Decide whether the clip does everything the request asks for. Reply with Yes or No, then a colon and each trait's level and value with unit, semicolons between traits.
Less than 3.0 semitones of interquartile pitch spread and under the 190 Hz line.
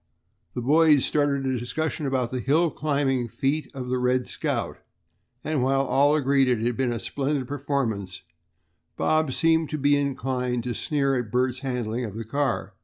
Yes: narrow, 2.5 semitones; low, 135 Hz